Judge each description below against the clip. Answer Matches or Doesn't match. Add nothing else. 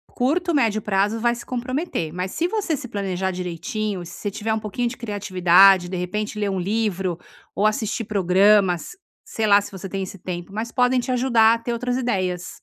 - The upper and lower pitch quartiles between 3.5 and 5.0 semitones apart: Matches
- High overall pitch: Matches